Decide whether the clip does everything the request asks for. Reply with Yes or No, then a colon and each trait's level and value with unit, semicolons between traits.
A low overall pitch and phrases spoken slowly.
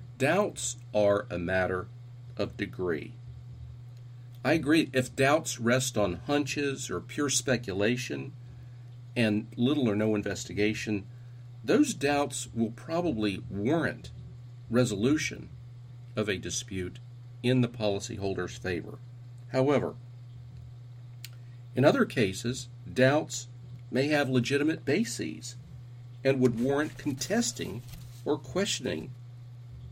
Yes: low, 120 Hz; slow, 100 wpm